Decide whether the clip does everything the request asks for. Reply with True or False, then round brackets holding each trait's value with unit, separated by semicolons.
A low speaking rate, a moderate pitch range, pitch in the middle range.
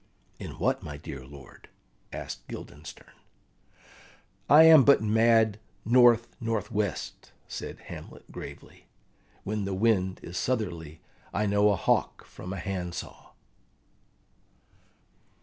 False (115 wpm; 4.2 semitones; 105 Hz)